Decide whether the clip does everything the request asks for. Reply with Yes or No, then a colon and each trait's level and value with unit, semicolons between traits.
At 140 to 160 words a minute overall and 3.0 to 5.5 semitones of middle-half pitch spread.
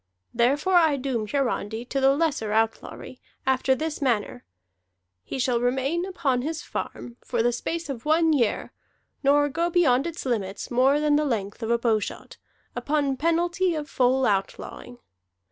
Yes: average, 155 wpm; average, 4.3 semitones